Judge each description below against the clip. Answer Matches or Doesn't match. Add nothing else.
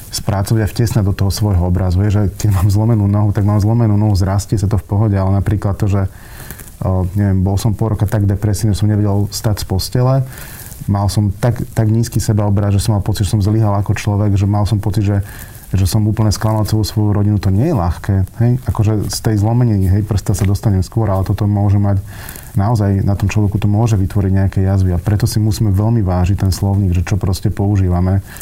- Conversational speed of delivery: Doesn't match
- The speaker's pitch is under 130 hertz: Matches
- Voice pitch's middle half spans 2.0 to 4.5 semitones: Doesn't match